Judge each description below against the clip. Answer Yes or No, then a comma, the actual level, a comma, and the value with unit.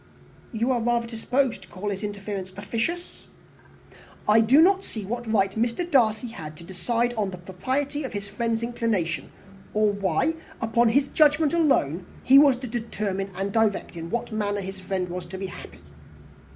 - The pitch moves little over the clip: No, average, 3.9 semitones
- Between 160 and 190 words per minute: Yes, average, 180 wpm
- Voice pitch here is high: Yes, high, 220 Hz